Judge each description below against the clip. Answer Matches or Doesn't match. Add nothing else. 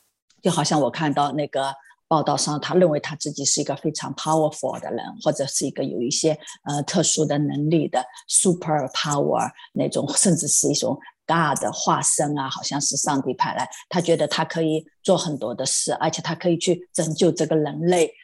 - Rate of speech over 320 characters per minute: Matches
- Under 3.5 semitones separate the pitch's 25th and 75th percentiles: Matches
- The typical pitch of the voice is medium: Matches